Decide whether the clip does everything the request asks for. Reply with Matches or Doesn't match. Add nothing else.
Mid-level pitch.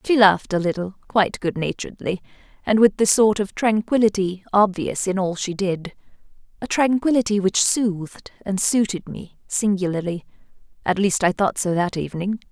Doesn't match